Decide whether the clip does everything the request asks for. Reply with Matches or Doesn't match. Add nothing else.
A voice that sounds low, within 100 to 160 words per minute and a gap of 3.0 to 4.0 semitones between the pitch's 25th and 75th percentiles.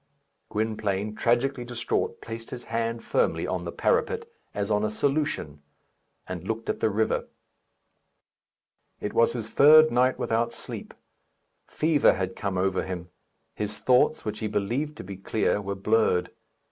Matches